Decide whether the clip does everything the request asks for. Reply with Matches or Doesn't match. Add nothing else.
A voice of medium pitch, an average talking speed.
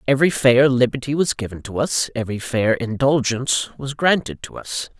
Doesn't match